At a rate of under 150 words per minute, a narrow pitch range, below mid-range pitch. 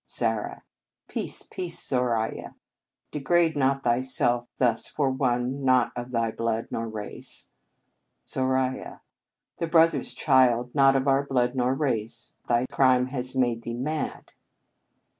Yes: slow, 135 wpm; narrow, 2.2 semitones; low, 130 Hz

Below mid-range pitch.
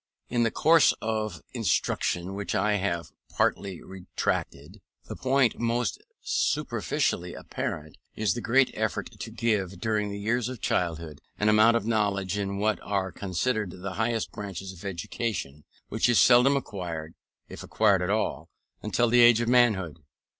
Yes: low, 105 Hz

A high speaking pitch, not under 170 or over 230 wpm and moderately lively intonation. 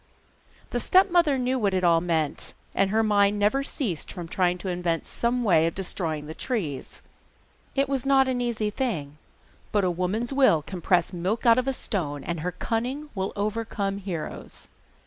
No: high, 200 Hz; average, 180 wpm; wide, 6.0 semitones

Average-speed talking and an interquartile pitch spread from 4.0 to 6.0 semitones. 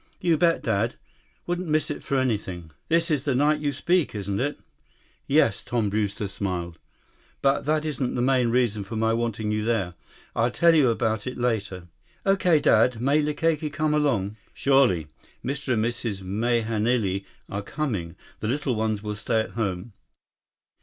Yes: average, 165 wpm; wide, 5.6 semitones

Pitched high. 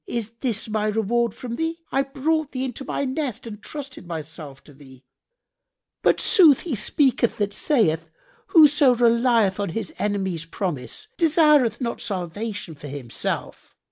Yes: high, 230 Hz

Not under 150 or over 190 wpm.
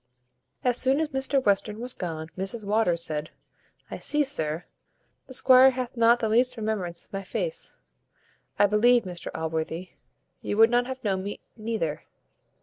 Yes: average, 160 wpm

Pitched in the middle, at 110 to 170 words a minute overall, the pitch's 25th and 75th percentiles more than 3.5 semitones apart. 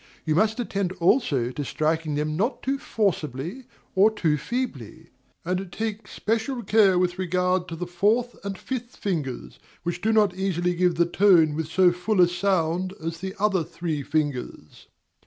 Yes: medium, 180 Hz; average, 165 wpm; average, 4.4 semitones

